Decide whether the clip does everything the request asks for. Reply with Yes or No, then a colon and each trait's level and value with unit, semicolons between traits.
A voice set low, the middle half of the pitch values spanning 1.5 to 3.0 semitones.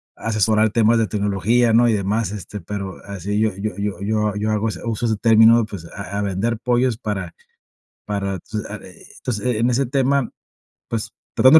Yes: low, 110 Hz; narrow, 2.4 semitones